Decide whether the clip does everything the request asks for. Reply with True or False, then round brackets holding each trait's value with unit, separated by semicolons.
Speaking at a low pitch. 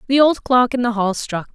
False (240 Hz)